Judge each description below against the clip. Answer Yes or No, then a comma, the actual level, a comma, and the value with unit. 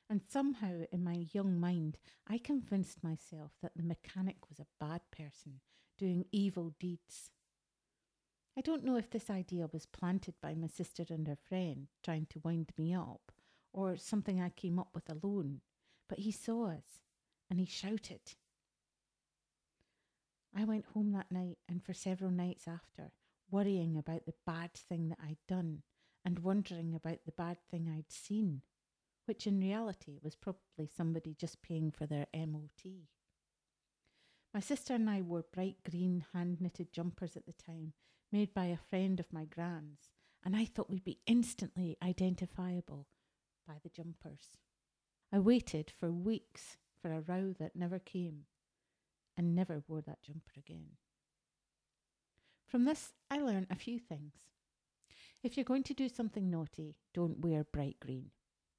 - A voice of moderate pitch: Yes, medium, 175 Hz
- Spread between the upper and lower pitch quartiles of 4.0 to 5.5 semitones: No, average, 3.4 semitones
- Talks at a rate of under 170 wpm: Yes, average, 155 wpm